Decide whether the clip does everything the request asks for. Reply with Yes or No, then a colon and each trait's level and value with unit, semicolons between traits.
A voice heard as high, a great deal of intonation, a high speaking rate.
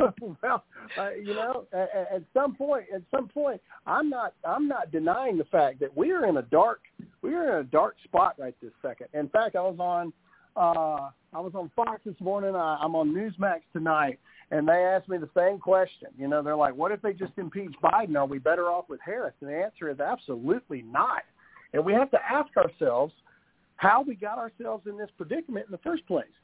Yes: high, 195 Hz; wide, 5.8 semitones; fast, 215 wpm